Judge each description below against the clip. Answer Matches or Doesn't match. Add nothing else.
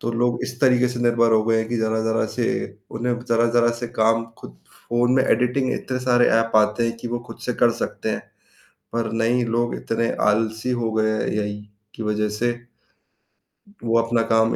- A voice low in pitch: Matches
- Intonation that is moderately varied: Doesn't match